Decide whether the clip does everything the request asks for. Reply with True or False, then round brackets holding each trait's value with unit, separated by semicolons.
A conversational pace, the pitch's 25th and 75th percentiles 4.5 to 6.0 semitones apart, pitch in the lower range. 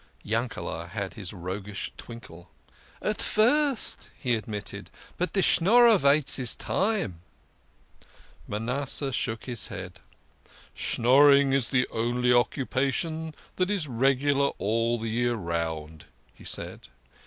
False (130 wpm; 5.5 semitones; 120 Hz)